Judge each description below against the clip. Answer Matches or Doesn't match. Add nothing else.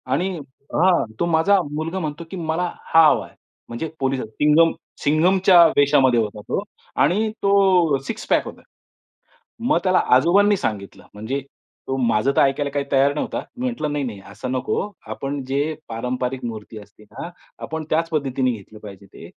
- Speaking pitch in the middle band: Matches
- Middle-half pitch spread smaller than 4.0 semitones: Doesn't match